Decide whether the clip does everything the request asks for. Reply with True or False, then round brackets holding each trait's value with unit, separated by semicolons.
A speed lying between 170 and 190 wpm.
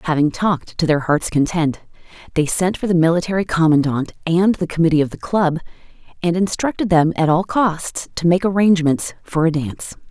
True (180 wpm)